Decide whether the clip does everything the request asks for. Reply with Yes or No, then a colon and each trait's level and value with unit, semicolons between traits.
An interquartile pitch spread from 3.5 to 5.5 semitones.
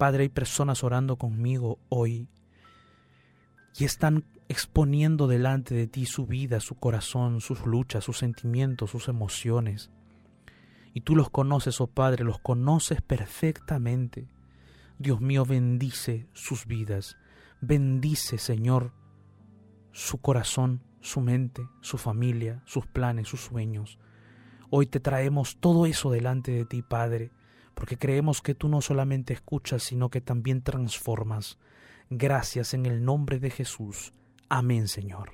No: average, 2.8 semitones